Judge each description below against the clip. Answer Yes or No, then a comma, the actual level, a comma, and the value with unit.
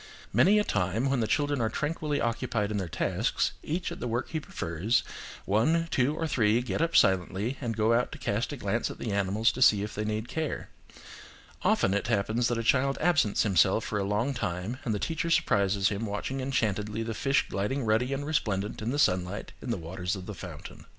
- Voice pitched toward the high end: No, low, 115 Hz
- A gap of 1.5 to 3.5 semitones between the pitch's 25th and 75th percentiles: No, average, 5.0 semitones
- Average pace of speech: No, fast, 210 wpm